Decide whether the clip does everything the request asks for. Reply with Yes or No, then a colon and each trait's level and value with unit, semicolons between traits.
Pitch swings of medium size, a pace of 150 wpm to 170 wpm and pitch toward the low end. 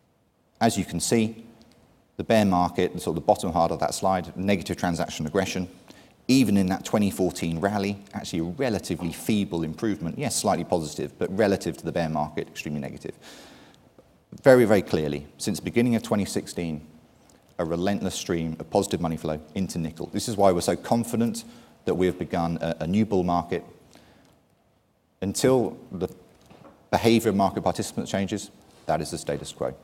Yes: average, 4.4 semitones; average, 165 wpm; very low, 95 Hz